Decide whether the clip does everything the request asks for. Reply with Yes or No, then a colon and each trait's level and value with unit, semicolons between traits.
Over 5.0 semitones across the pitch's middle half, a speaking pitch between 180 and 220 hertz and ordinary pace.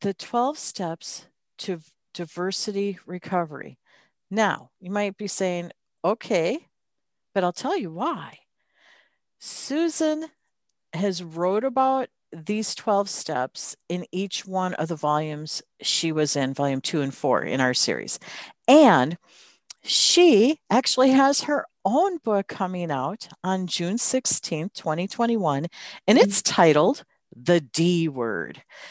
No: wide, 5.5 semitones; medium, 185 Hz; slow, 120 wpm